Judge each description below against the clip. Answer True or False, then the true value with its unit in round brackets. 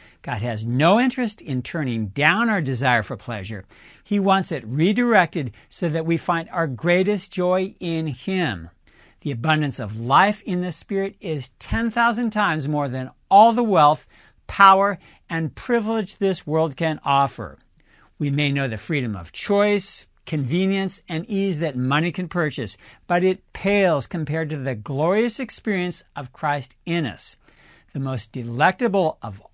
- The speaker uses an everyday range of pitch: False (6.6 semitones)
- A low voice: False (160 Hz)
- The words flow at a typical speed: True (155 wpm)